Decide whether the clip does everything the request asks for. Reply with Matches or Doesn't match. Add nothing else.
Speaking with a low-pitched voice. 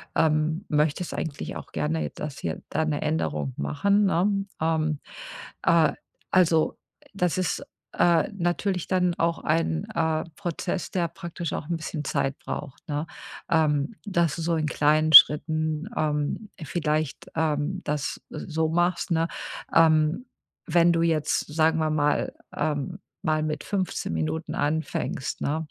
Doesn't match